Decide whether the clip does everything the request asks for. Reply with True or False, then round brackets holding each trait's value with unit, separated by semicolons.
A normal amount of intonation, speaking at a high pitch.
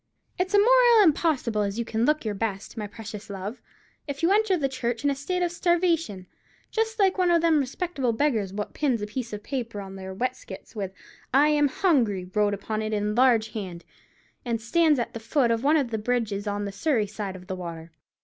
False (6.7 semitones; 235 Hz)